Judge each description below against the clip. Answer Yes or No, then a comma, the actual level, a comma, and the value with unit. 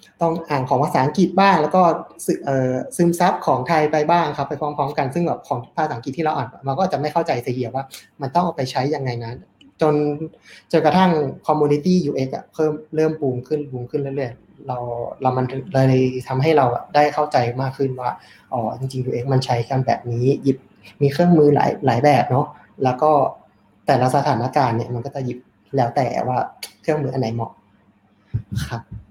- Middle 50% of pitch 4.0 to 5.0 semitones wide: No, average, 3.2 semitones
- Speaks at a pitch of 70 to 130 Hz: No, medium, 140 Hz